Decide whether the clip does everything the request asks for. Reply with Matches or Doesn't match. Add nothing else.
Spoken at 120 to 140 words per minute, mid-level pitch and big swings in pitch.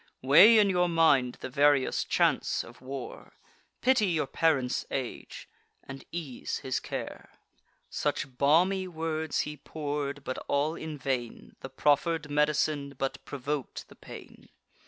Doesn't match